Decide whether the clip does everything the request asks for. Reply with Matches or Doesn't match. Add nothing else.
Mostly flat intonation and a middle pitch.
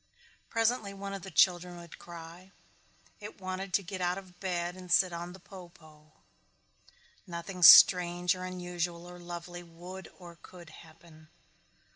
Matches